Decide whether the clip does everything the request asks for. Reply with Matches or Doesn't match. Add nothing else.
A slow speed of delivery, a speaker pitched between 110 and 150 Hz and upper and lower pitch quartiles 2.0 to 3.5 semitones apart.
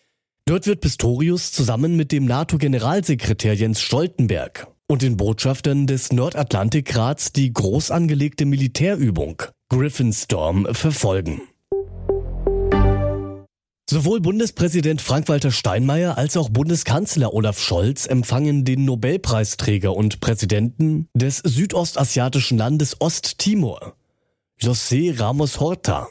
Doesn't match